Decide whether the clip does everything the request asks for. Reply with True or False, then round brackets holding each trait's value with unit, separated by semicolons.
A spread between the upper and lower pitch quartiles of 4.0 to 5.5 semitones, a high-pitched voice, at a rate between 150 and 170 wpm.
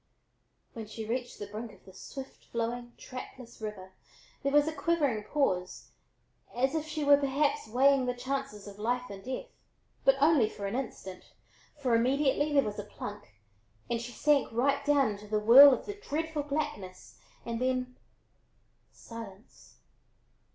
True (4.8 semitones; 250 Hz; 160 wpm)